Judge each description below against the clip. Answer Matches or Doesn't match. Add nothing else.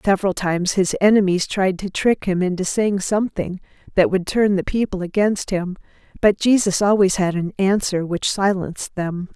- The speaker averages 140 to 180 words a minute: Matches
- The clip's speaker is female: Matches